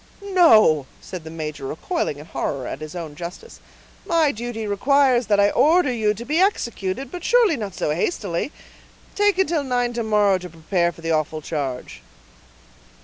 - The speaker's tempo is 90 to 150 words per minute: No, average, 170 wpm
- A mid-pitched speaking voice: No, high, 210 Hz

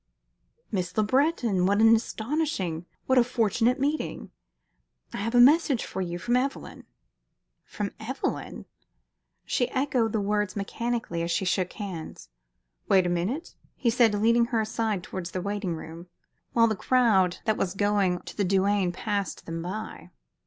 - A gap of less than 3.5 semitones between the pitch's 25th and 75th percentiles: No, average, 4.4 semitones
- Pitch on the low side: No, high, 210 Hz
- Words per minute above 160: No, average, 155 wpm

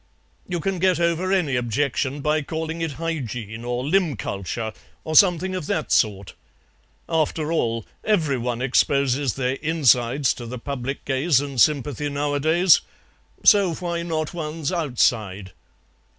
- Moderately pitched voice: Yes, medium, 145 Hz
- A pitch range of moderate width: Yes, average, 4.9 semitones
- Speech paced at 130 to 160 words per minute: Yes, slow, 135 wpm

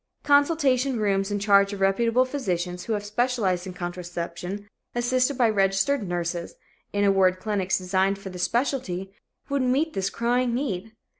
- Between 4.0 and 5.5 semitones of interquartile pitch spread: Yes, average, 5.1 semitones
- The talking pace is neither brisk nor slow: Yes, average, 155 wpm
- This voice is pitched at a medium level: No, high, 205 Hz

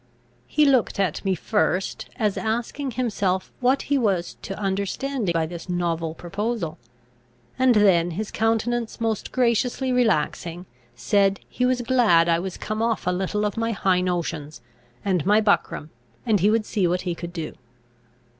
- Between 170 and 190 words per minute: No, average, 160 wpm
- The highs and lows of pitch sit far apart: No, average, 4.6 semitones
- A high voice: Yes, high, 200 Hz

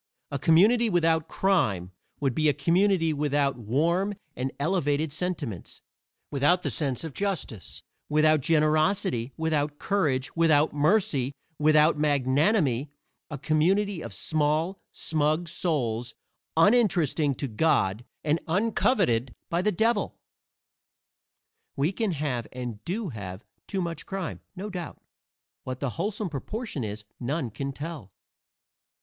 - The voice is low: No, medium, 155 Hz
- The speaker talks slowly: Yes, slow, 120 wpm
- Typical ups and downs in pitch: Yes, average, 4.7 semitones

